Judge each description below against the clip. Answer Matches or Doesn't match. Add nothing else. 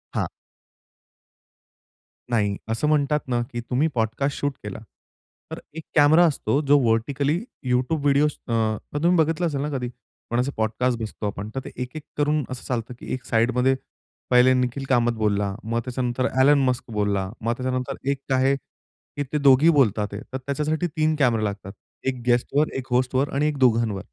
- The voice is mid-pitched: Doesn't match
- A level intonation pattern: Doesn't match